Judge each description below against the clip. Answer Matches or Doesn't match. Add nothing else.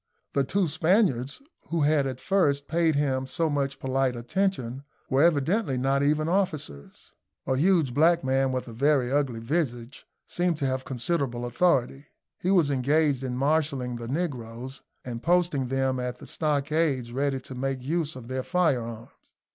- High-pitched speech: Doesn't match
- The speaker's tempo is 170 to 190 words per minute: Doesn't match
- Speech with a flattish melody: Doesn't match